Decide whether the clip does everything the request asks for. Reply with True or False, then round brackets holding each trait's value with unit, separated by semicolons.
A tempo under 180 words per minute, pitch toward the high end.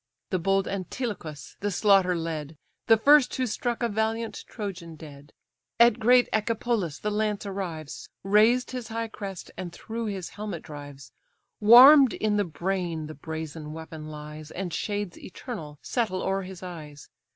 True (150 wpm; 195 Hz)